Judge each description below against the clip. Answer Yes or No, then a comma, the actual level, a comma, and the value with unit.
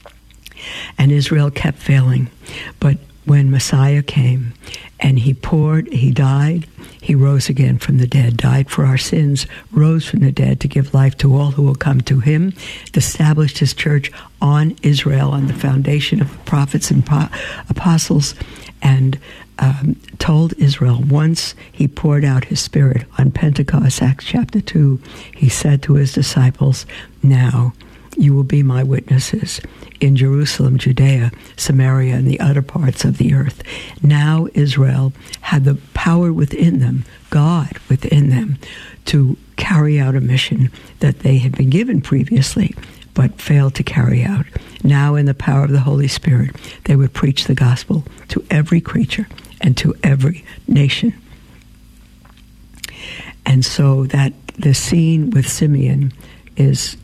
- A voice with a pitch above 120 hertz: Yes, medium, 140 Hz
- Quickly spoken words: No, average, 150 wpm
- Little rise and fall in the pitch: Yes, narrow, 2.2 semitones